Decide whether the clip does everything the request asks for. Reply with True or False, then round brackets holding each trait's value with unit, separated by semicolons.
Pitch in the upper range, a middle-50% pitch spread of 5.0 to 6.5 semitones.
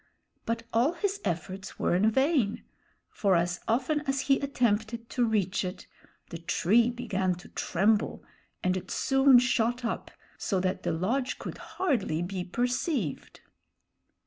True (225 Hz; 5.3 semitones)